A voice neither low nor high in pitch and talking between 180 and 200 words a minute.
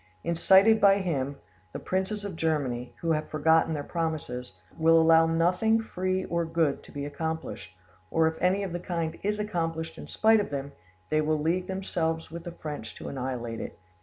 Yes: medium, 165 Hz; average, 185 wpm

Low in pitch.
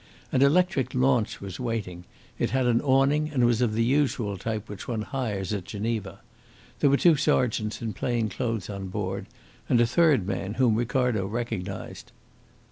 Yes: low, 115 Hz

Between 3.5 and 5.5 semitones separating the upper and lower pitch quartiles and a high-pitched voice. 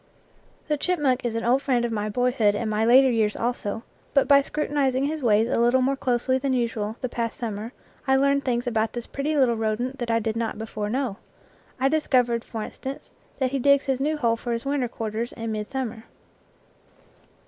No: average, 3.1 semitones; high, 245 Hz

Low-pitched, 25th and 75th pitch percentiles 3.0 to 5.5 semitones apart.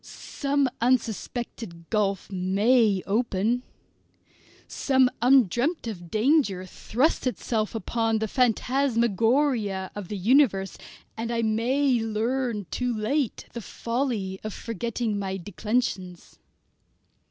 No: high, 225 Hz; average, 3.7 semitones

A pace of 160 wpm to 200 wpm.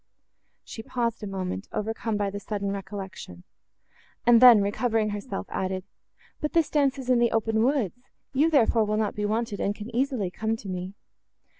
Yes: average, 170 wpm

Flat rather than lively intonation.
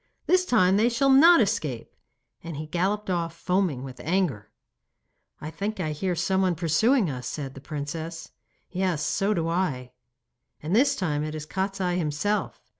No: average, 4.5 semitones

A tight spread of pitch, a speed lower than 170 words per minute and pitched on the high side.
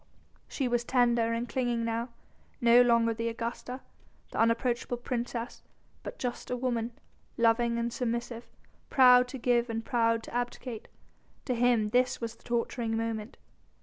Yes: narrow, 1.2 semitones; average, 150 wpm; high, 235 Hz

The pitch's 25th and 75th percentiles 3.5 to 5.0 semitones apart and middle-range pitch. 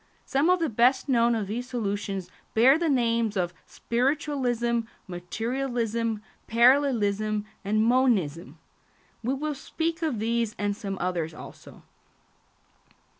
No: average, 4.2 semitones; high, 235 Hz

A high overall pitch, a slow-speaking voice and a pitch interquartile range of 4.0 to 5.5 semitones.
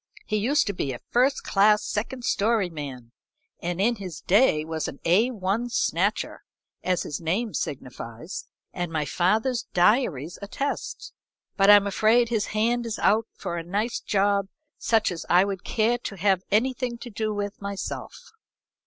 No: high, 200 Hz; average, 160 wpm; average, 4.4 semitones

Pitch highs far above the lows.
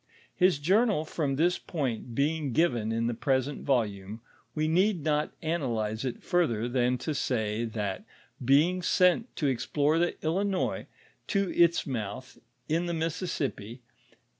Yes: wide, 6.2 semitones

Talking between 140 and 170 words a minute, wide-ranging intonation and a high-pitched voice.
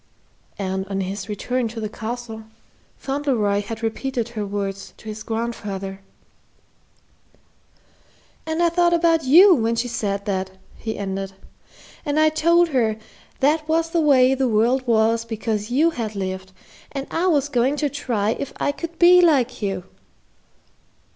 Yes: average, 150 wpm; wide, 5.9 semitones; high, 235 Hz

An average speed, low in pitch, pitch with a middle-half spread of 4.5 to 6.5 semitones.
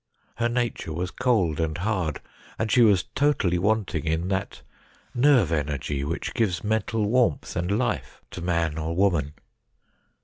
Yes: average, 145 wpm; very low, 90 Hz; wide, 5.4 semitones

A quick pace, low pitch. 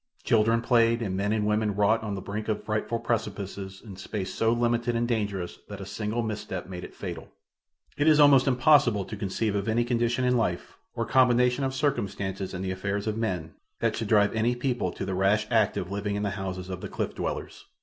Yes: fast, 220 wpm; low, 110 Hz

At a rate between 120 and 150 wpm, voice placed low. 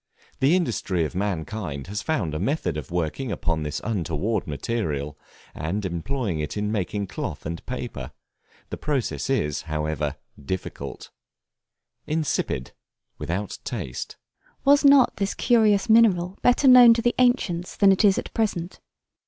Yes: average, 140 wpm; low, 105 Hz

